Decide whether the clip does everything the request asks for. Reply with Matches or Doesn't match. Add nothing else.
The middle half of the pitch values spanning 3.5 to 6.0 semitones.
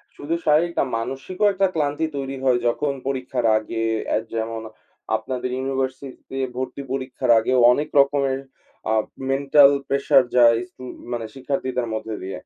Doesn't match